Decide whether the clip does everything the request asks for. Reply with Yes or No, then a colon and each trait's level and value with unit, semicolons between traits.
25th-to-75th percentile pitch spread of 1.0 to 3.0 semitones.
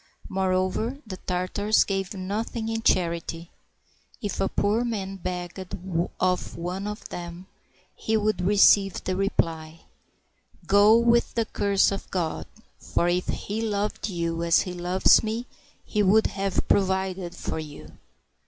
Yes: average, 2.7 semitones